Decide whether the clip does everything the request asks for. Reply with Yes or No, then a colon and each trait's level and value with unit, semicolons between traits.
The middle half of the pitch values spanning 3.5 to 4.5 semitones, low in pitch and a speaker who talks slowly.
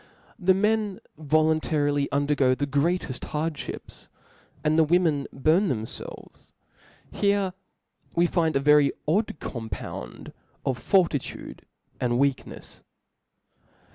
No: average, 4.0 semitones; medium, 155 Hz; slow, 100 wpm